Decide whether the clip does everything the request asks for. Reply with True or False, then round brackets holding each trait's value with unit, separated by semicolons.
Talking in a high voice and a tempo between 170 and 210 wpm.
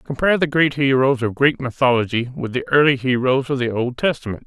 False (130 Hz; 200 wpm)